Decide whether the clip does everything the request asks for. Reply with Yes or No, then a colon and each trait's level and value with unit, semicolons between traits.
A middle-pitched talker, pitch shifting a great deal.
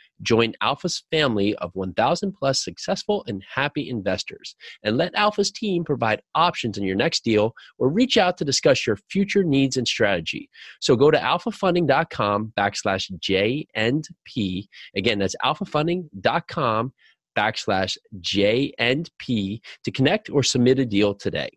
No: low, 130 Hz; wide, 8.8 semitones